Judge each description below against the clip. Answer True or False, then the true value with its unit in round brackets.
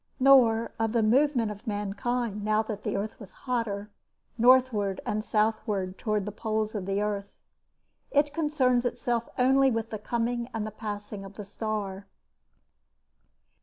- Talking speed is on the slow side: False (150 wpm)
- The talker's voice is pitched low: False (220 Hz)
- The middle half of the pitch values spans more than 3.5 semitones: False (2.8 semitones)